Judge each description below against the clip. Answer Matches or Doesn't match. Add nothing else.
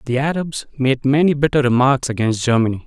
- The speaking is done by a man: Matches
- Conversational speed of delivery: Matches